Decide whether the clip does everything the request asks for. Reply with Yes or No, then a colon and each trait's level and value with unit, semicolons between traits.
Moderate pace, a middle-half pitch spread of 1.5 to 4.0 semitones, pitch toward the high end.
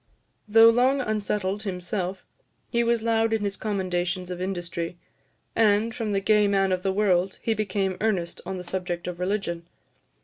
Yes: average, 165 wpm; average, 3.1 semitones; high, 195 Hz